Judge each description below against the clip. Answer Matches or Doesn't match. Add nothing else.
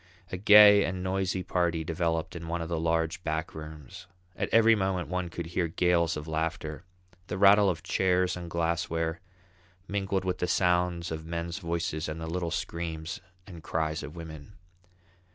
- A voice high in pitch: Doesn't match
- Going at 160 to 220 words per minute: Matches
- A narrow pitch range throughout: Matches